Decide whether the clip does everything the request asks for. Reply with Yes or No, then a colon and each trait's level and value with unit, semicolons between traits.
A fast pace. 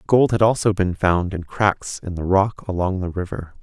Yes: fast, 215 wpm